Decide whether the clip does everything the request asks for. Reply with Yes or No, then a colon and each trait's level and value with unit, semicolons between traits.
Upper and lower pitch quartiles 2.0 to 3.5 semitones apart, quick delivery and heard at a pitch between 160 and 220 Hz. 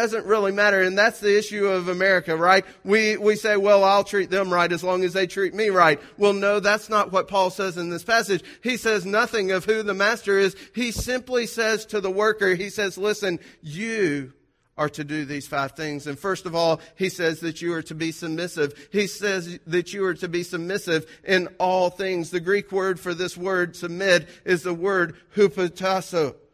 Yes: average, 2.7 semitones; fast, 210 wpm; high, 190 Hz